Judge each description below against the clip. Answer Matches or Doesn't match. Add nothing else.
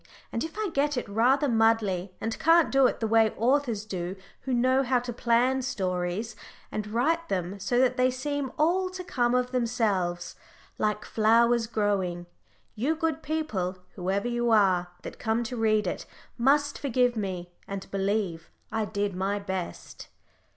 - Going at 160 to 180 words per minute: Matches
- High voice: Matches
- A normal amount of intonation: Matches